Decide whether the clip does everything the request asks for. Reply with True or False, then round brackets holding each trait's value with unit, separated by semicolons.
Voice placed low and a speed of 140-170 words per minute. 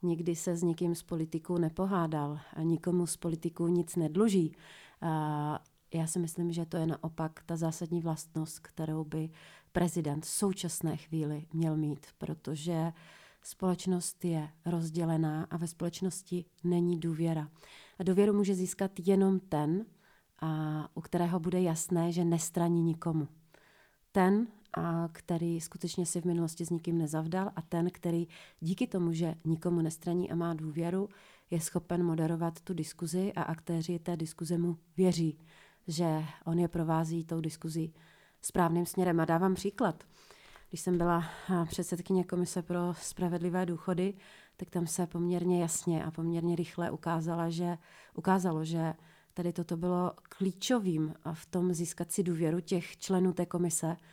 False (170 Hz; 145 wpm)